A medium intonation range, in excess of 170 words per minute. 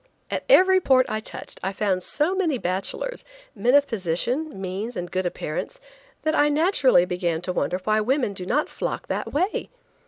No: wide, 8.5 semitones; average, 180 wpm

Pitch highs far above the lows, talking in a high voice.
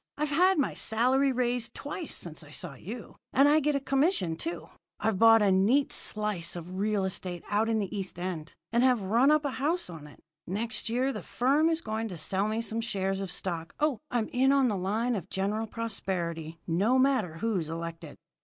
Yes: wide, 5.9 semitones; high, 220 Hz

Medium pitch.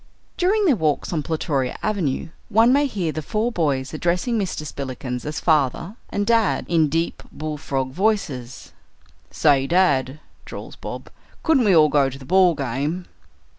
Yes: medium, 160 Hz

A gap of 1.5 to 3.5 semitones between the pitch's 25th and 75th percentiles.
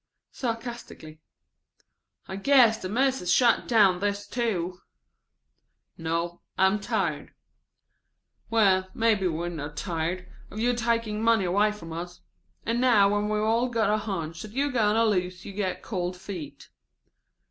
No: average, 4.3 semitones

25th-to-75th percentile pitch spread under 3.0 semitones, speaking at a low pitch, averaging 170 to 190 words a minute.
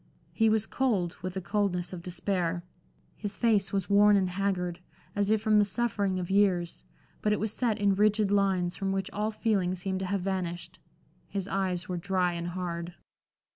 No: narrow, 2.4 semitones; high, 195 Hz; average, 185 wpm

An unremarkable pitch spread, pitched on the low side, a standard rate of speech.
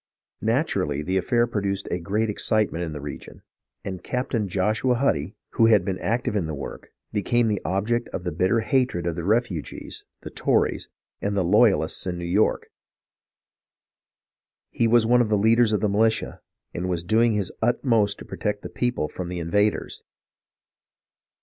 Yes: average, 4.2 semitones; low, 105 Hz; average, 170 wpm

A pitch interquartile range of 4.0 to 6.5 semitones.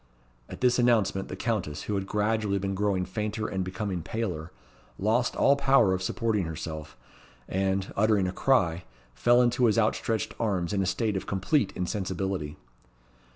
No: average, 3.4 semitones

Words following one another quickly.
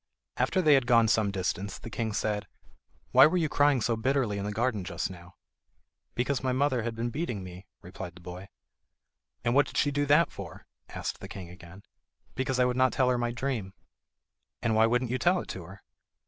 Yes: fast, 210 wpm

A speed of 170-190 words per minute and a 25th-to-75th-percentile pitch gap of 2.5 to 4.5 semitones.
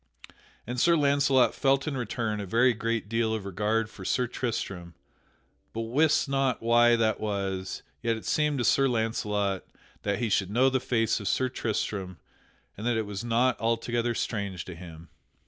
Yes: average, 175 wpm; average, 3.4 semitones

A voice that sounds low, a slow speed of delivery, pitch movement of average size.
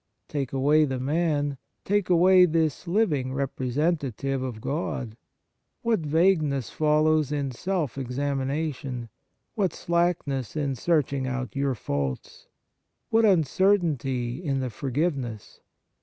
No: medium, 145 Hz; slow, 110 wpm; average, 4.2 semitones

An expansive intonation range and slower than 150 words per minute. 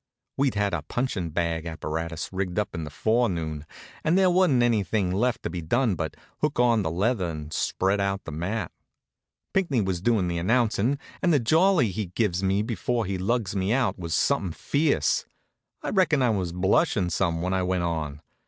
No: wide, 5.8 semitones; average, 190 wpm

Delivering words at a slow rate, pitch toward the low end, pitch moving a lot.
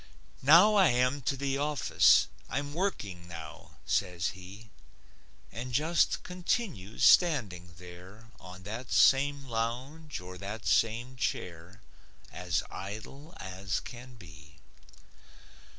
Yes: slow, 110 wpm; low, 115 Hz; wide, 7.4 semitones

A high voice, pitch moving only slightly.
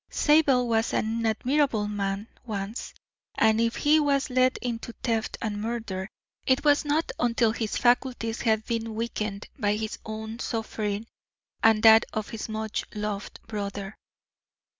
Yes: high, 225 Hz; narrow, 2.3 semitones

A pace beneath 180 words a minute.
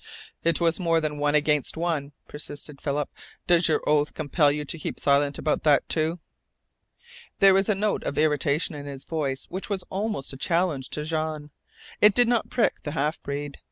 No: average, 190 wpm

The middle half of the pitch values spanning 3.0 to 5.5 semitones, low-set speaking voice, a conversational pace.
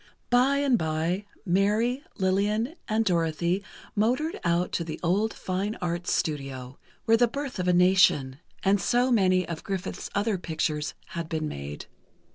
No: average, 5.0 semitones; medium, 185 Hz; average, 150 wpm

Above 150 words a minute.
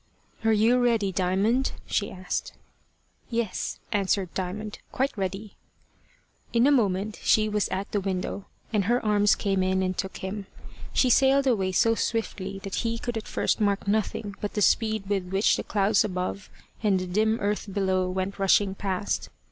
Yes: average, 170 wpm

